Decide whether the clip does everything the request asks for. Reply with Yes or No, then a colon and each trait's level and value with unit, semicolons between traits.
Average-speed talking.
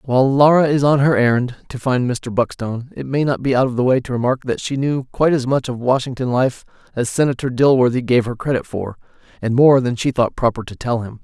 No: fast, 240 wpm